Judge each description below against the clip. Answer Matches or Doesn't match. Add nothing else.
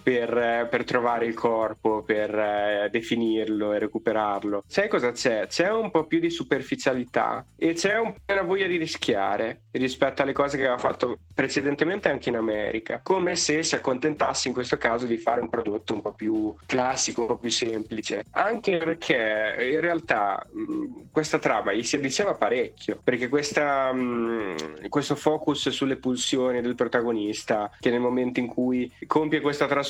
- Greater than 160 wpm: Matches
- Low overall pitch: Matches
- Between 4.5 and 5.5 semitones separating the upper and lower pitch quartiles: Matches